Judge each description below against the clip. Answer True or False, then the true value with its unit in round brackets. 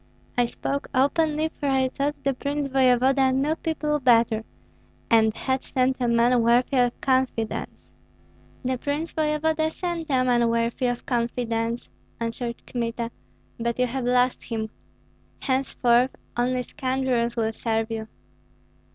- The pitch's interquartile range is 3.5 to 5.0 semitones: False (2.7 semitones)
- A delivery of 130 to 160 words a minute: True (135 wpm)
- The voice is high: True (250 Hz)